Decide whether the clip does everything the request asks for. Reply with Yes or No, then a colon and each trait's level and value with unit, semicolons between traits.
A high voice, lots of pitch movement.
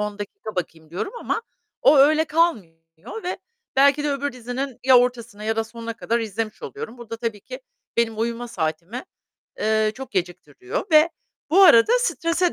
Yes: high, 235 Hz; wide, 5.9 semitones